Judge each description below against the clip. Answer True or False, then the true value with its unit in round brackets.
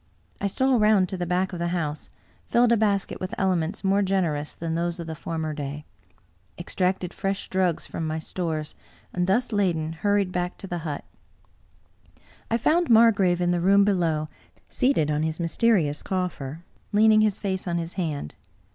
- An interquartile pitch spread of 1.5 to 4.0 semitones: True (3.6 semitones)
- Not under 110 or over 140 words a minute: False (175 wpm)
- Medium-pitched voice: True (180 Hz)